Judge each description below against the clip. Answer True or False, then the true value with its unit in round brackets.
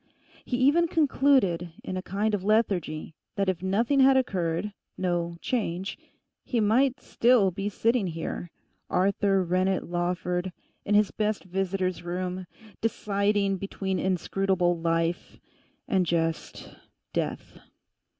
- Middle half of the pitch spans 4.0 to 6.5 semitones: False (3.2 semitones)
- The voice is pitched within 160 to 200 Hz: True (190 Hz)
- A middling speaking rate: False (115 wpm)